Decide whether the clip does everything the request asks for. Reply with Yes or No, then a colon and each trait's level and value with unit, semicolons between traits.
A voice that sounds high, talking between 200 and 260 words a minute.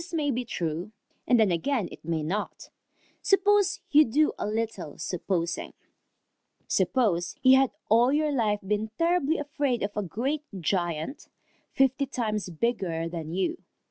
No: high, 225 Hz; average, 145 wpm